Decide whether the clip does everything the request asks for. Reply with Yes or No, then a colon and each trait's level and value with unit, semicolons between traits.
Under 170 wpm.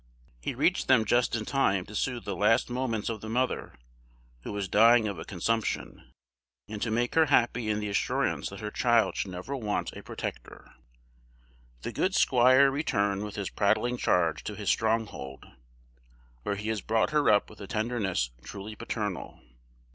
No: average, 175 wpm